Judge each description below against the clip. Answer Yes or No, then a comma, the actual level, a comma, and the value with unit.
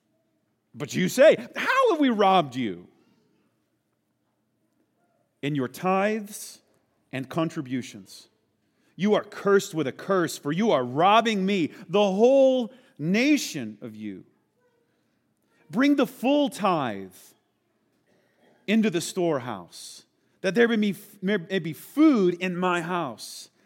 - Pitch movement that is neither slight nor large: No, wide, 7.3 semitones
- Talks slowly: Yes, slow, 120 wpm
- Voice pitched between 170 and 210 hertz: Yes, high, 190 Hz